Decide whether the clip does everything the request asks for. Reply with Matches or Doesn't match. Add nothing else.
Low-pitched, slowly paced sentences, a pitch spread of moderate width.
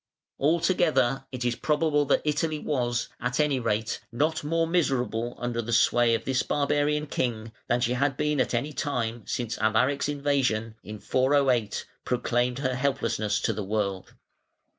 Doesn't match